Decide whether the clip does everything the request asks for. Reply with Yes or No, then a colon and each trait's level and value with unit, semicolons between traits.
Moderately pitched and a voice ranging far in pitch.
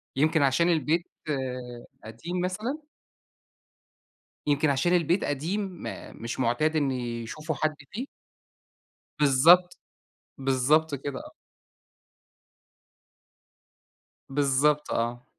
No: medium, 145 Hz; average, 4.3 semitones